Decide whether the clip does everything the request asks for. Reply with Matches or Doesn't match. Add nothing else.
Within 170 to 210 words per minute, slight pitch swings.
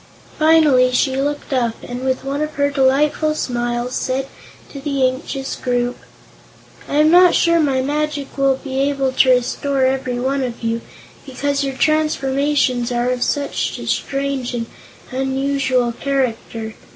Doesn't match